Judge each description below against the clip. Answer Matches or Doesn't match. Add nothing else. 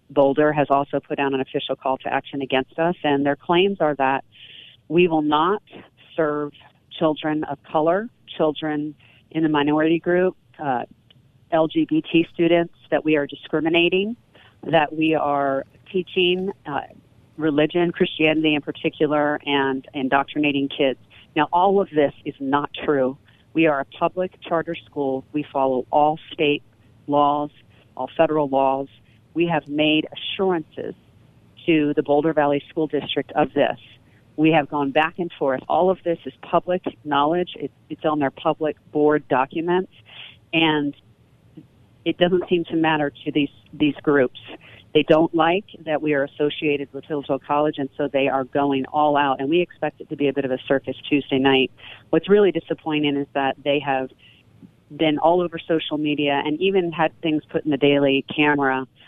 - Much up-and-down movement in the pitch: Doesn't match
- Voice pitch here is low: Doesn't match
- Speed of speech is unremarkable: Matches